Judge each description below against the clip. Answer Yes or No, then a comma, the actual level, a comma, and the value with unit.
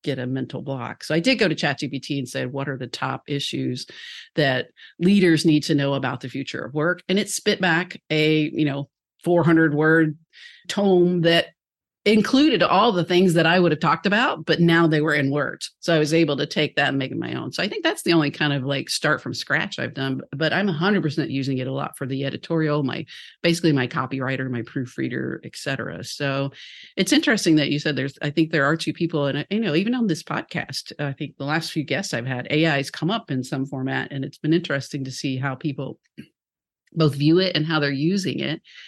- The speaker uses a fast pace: Yes, fast, 230 wpm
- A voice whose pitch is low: No, medium, 155 Hz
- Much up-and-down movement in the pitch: No, average, 3.6 semitones